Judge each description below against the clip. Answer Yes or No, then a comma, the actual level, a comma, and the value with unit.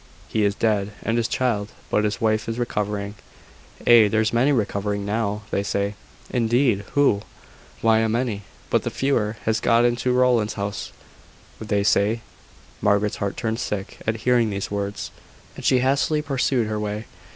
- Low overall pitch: Yes, low, 110 Hz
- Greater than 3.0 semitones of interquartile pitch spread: No, narrow, 2.6 semitones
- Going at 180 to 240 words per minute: No, average, 160 wpm